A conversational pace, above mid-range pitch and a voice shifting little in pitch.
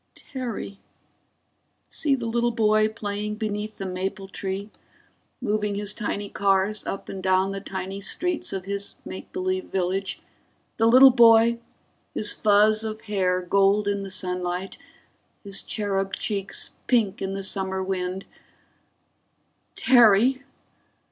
No: slow, 130 wpm; high, 200 Hz; narrow, 2.3 semitones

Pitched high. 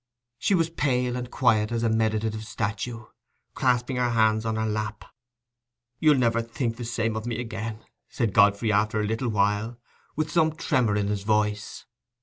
No: low, 115 Hz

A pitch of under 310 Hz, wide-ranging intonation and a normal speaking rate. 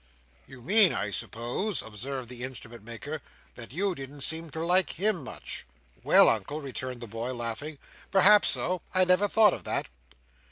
Yes: medium, 140 Hz; wide, 7.2 semitones; average, 165 wpm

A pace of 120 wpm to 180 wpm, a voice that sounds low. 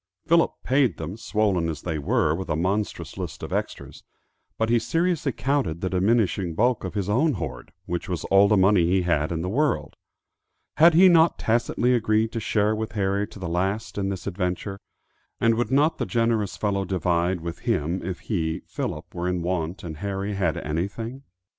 No: average, 190 wpm; low, 100 Hz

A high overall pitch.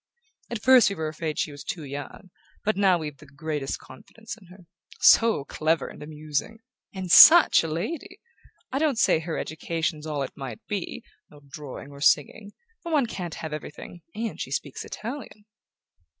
No: medium, 165 Hz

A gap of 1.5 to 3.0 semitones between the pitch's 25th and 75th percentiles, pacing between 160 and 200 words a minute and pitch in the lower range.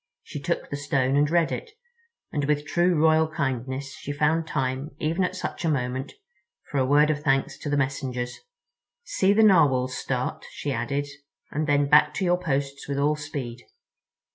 No: narrow, 2.6 semitones; average, 180 wpm; medium, 145 Hz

